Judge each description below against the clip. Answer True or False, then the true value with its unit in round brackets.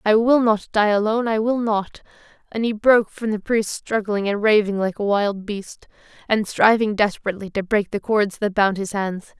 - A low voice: False (210 Hz)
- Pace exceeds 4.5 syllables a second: True (5.1 syllables/s)